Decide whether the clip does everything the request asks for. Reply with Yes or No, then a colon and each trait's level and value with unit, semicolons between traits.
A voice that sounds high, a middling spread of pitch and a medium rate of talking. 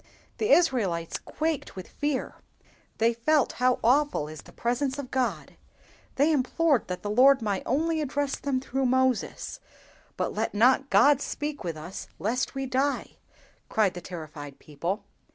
No: very high, 255 Hz; wide, 6.0 semitones; average, 150 wpm